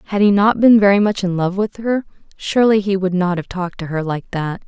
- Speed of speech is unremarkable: No, fast, 255 wpm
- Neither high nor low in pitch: No, high, 195 Hz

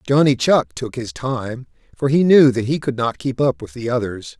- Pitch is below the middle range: Yes, low, 130 Hz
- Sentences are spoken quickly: Yes, fast, 230 wpm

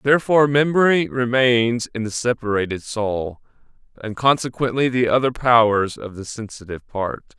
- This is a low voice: Yes, low, 120 Hz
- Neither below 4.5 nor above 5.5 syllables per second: Yes, 5.0 syllables/s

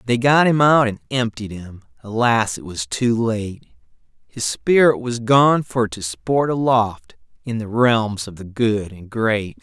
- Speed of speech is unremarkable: Yes, average, 175 wpm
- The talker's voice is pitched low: Yes, low, 115 Hz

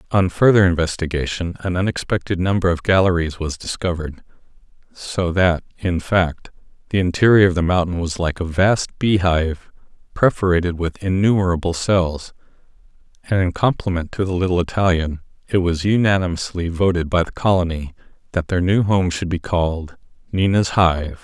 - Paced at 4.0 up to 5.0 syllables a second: No, 5.2 syllables/s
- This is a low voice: Yes, very low, 90 Hz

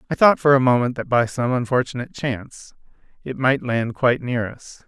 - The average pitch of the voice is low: Yes, low, 125 Hz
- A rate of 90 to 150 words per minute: No, average, 195 wpm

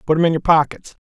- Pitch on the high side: No, medium, 160 Hz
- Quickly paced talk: Yes, fast, 280 wpm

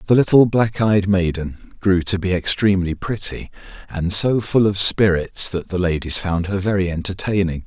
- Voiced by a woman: No, male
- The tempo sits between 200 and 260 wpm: No, average, 170 wpm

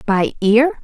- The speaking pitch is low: No, high, 225 Hz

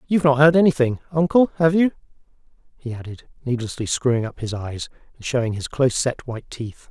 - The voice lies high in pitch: No, low, 135 Hz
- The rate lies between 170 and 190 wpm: Yes, average, 180 wpm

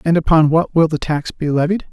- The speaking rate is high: Yes, fast, 250 wpm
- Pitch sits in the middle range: Yes, medium, 160 Hz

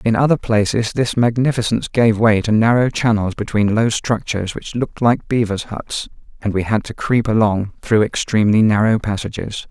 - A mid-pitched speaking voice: No, low, 110 Hz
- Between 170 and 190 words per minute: Yes, average, 175 wpm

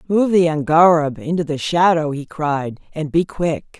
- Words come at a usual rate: Yes, average, 175 wpm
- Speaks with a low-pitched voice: No, medium, 160 Hz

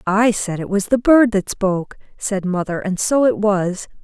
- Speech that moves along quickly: Yes, fast, 210 wpm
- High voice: Yes, high, 205 Hz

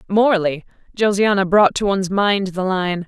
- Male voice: No, female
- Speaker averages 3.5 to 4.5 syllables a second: No, 5.5 syllables/s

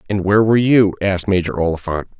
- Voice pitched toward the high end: No, low, 100 Hz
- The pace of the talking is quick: No, average, 190 wpm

